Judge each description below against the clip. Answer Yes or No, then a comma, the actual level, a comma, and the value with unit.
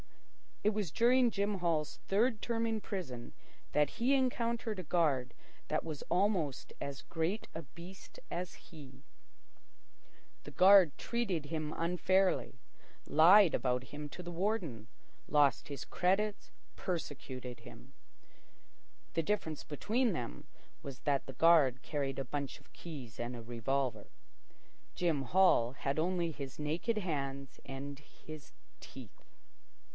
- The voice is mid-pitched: Yes, medium, 160 Hz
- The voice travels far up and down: Yes, wide, 5.8 semitones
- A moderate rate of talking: No, slow, 130 wpm